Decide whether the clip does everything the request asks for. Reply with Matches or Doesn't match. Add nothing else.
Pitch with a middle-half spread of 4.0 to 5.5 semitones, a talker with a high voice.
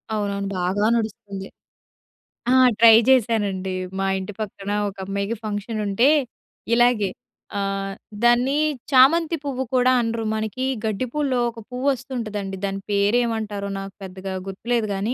Doesn't match